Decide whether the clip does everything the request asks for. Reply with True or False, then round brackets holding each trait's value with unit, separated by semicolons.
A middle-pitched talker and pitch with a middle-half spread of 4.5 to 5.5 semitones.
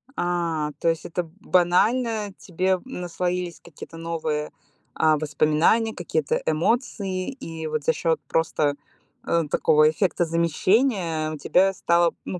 False (170 Hz; 2.9 semitones)